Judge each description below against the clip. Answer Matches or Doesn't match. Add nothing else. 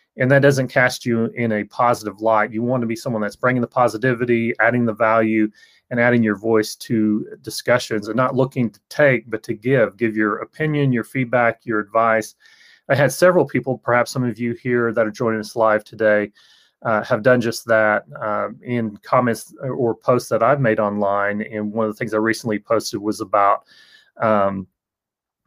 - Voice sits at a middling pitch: Doesn't match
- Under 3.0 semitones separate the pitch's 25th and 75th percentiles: Matches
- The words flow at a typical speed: Matches